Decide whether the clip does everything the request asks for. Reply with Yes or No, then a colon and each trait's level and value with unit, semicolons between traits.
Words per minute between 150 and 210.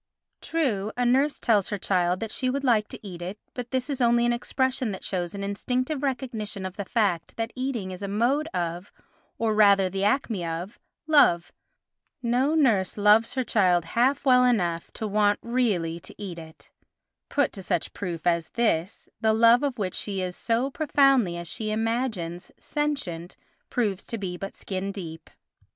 Yes: average, 175 wpm